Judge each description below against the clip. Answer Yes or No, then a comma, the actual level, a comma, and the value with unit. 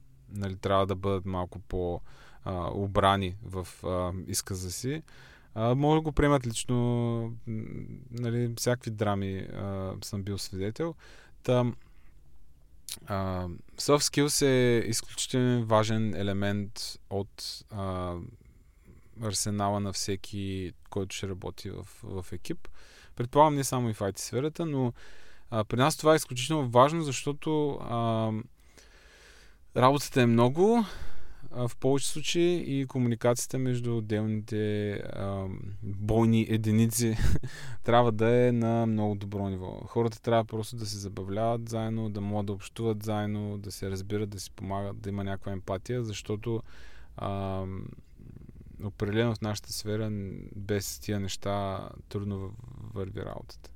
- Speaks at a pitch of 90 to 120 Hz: Yes, low, 110 Hz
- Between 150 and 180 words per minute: No, average, 125 wpm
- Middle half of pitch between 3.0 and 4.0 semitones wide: Yes, average, 3.6 semitones